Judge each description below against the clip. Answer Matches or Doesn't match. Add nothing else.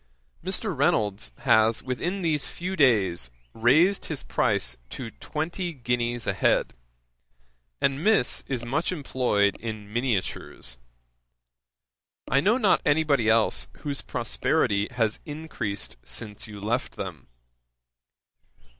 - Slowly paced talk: Matches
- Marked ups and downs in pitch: Matches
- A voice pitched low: Matches